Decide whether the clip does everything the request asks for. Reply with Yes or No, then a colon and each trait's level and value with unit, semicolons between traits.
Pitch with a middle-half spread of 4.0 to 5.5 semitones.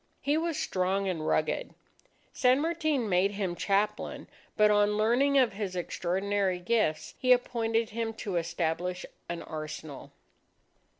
Yes: average, 4.7 semitones